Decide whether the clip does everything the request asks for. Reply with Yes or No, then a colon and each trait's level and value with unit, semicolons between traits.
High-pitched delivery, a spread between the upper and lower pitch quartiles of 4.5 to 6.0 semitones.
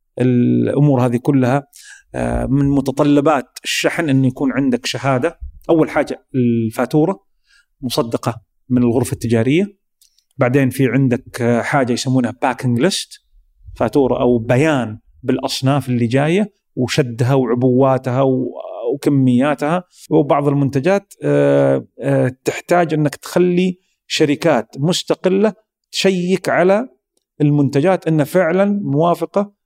No: medium, 140 Hz; average, 5.2 semitones